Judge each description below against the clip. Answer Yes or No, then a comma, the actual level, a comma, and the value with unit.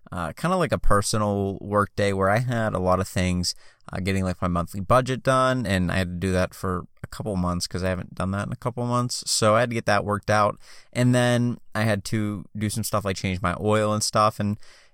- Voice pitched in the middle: No, low, 105 Hz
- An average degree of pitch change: Yes, average, 3.5 semitones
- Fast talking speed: Yes, fast, 255 wpm